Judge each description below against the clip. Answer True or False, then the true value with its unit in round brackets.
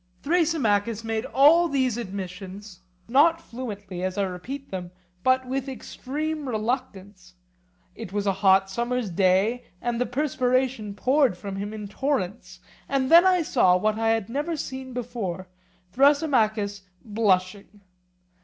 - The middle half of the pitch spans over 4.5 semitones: True (5.1 semitones)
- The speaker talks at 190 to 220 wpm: False (135 wpm)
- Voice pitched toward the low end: False (225 Hz)